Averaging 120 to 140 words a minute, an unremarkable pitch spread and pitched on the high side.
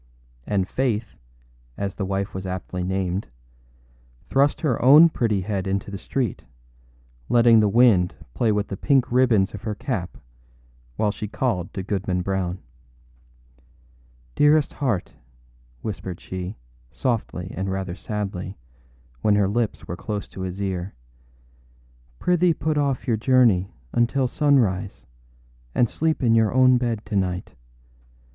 No: slow, 135 wpm; average, 4.6 semitones; low, 105 Hz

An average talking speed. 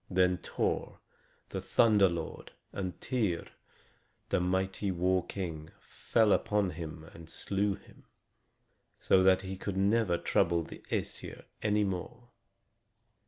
No: slow, 120 wpm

